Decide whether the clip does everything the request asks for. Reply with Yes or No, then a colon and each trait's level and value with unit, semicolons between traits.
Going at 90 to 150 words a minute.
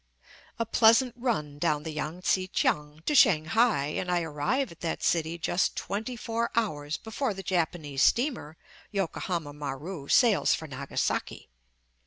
Yes: average, 145 wpm